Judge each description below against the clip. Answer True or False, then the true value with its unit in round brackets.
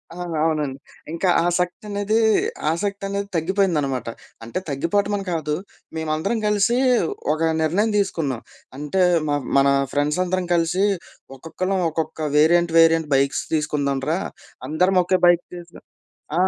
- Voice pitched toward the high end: False (170 Hz)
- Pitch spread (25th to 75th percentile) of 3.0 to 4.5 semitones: True (4.1 semitones)